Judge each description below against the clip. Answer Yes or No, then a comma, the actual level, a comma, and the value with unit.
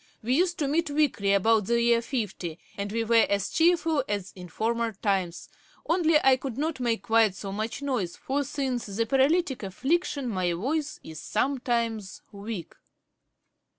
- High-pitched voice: Yes, high, 230 Hz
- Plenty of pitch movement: Yes, wide, 5.8 semitones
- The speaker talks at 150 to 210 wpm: Yes, average, 160 wpm